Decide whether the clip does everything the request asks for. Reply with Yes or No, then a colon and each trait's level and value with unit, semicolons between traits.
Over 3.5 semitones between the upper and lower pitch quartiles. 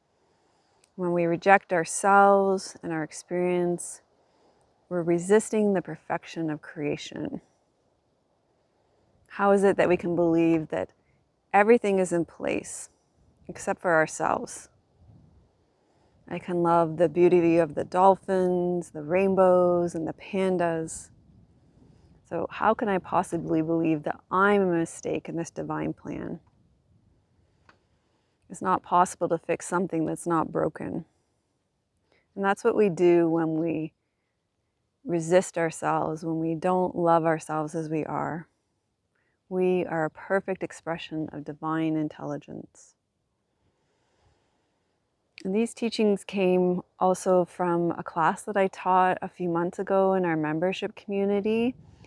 No: average, 2.8 semitones